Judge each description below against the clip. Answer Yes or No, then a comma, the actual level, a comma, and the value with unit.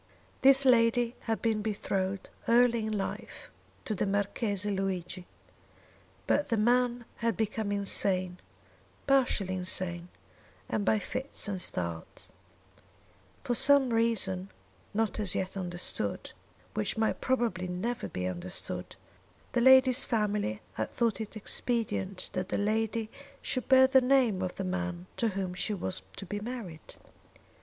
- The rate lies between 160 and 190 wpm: No, slow, 135 wpm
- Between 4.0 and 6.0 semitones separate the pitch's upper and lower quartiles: Yes, average, 4.3 semitones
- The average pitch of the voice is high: Yes, high, 210 Hz